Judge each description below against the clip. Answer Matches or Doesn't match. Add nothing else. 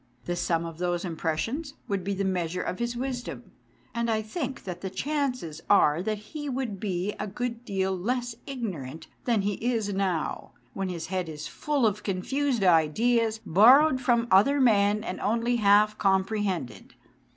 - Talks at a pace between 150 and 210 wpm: Matches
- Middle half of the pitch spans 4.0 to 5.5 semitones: Matches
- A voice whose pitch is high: Matches